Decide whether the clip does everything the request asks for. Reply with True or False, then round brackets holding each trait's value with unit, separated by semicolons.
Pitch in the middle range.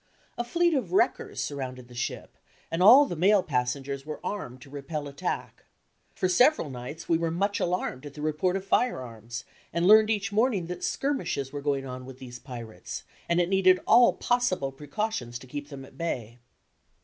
True (155 Hz)